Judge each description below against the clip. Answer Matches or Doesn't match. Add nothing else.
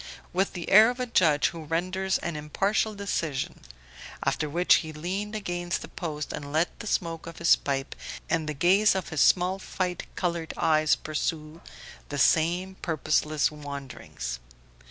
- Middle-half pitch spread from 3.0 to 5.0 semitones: Matches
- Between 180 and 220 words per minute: Doesn't match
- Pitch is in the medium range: Matches